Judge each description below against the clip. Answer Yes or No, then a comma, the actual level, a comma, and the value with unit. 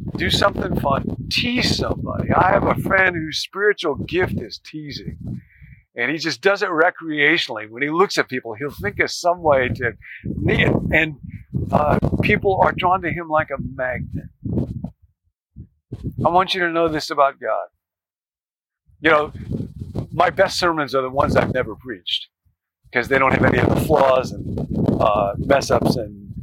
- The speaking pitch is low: No, medium, 145 Hz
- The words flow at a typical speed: Yes, average, 170 wpm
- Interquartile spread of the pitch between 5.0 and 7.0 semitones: Yes, wide, 5.6 semitones